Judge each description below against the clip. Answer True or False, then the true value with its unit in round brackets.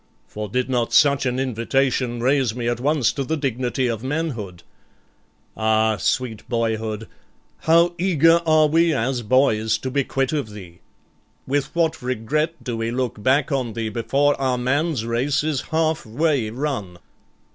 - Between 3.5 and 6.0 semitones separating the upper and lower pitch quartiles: True (4.3 semitones)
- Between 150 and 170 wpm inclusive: True (155 wpm)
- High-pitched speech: False (130 Hz)